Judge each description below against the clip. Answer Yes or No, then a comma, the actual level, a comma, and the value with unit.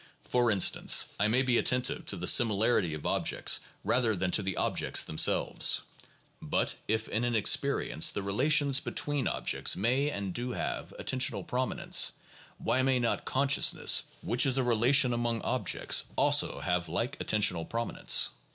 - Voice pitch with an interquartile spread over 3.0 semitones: Yes, average, 4.3 semitones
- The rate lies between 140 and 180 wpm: Yes, average, 155 wpm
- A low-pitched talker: Yes, low, 120 Hz